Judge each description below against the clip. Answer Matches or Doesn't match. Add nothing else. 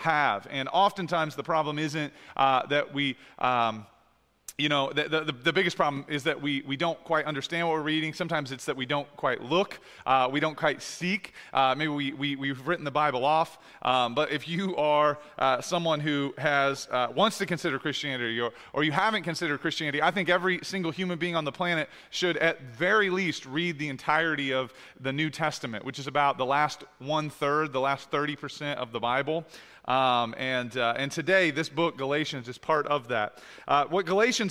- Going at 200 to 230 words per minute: Matches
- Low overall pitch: Doesn't match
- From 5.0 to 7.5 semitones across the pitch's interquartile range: Doesn't match